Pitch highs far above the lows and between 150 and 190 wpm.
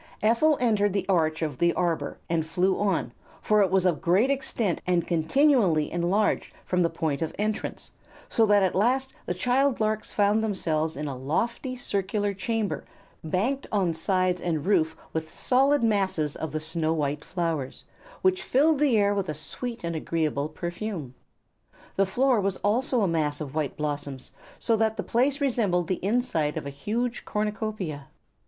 Yes: wide, 5.7 semitones; average, 170 wpm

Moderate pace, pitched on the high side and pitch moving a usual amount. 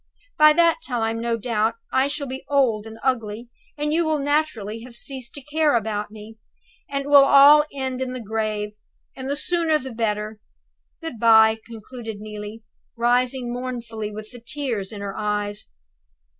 Yes: average, 170 wpm; high, 235 Hz; average, 4.3 semitones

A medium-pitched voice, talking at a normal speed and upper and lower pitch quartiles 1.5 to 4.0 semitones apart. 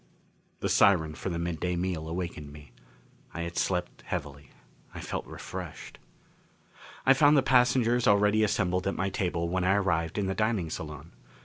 No: very low, 90 Hz; average, 165 wpm; average, 3.7 semitones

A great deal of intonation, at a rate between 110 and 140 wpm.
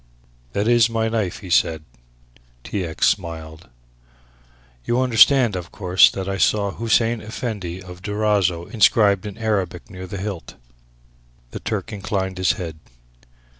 No: average, 3.4 semitones; slow, 135 wpm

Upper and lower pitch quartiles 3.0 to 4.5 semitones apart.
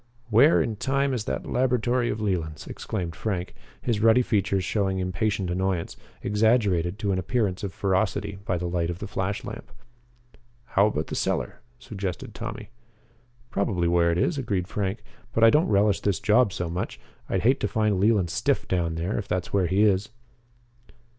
Yes: average, 3.3 semitones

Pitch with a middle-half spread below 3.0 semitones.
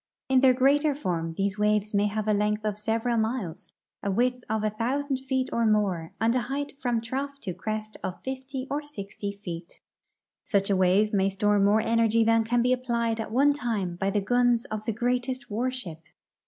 No: average, 3.6 semitones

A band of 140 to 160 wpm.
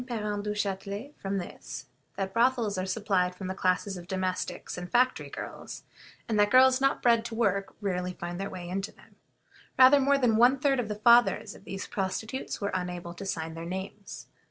No: average, 195 wpm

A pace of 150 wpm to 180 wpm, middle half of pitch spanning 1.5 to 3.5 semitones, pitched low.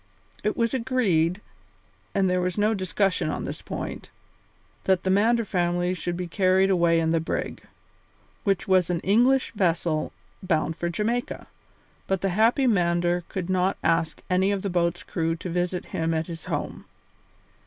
No: average, 165 wpm; narrow, 2.6 semitones; medium, 180 Hz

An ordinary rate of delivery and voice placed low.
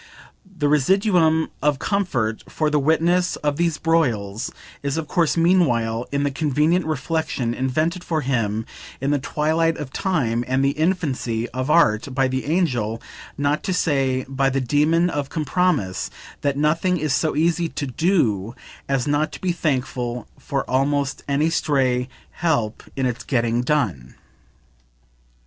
No: average, 150 wpm; medium, 145 Hz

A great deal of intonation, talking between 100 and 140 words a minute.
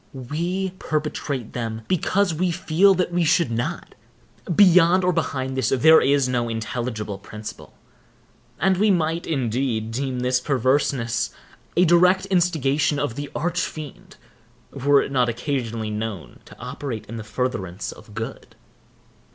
Yes: wide, 6.5 semitones; slow, 135 wpm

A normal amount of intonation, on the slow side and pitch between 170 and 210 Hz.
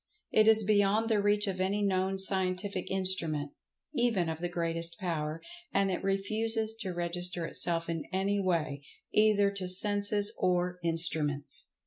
No: average, 3.1 semitones; average, 145 wpm; medium, 185 Hz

